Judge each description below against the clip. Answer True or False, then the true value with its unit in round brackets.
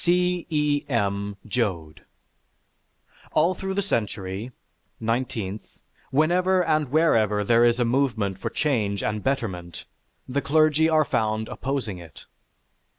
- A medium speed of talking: False (120 wpm)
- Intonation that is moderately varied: False (6.9 semitones)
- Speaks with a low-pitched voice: True (120 Hz)